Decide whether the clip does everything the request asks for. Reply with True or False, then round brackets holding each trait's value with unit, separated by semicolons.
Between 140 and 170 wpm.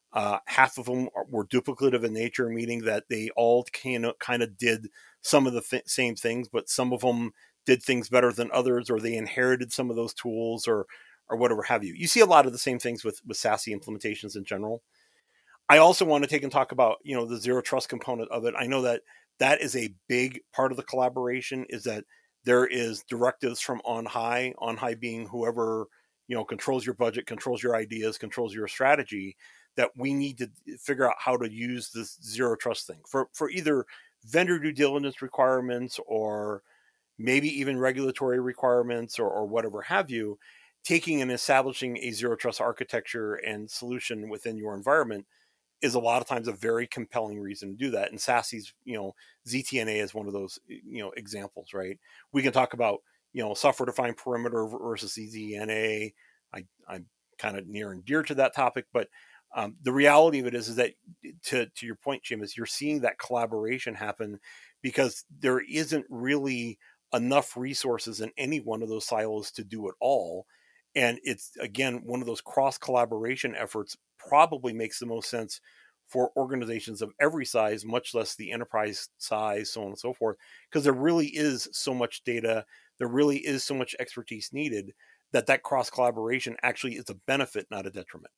False (195 wpm)